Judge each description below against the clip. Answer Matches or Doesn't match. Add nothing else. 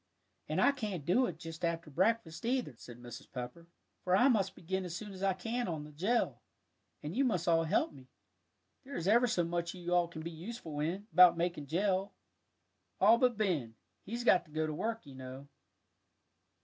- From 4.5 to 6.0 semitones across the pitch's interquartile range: Matches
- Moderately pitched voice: Matches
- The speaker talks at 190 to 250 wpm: Matches